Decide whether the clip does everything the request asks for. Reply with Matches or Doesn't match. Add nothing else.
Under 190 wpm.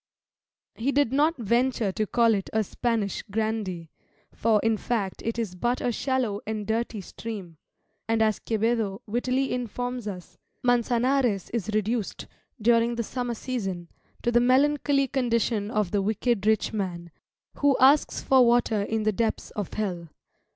Matches